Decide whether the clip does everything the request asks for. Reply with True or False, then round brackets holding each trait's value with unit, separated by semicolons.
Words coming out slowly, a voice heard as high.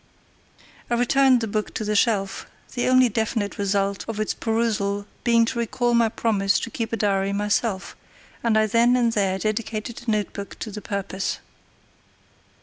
False (165 wpm; 215 Hz)